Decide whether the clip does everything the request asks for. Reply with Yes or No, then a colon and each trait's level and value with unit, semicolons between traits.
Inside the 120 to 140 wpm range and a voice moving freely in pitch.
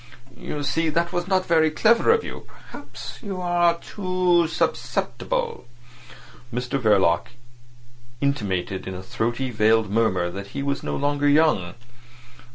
Yes: slow, 135 wpm; wide, 8.1 semitones